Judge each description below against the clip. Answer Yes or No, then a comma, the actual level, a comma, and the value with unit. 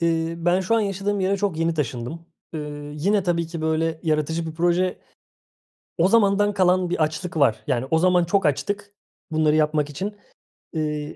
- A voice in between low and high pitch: Yes, medium, 165 Hz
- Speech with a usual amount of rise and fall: Yes, average, 3.4 semitones